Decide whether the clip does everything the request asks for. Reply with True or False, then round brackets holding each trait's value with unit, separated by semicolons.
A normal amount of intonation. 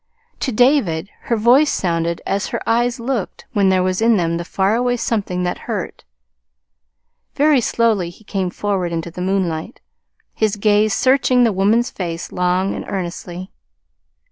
True (4.5 semitones)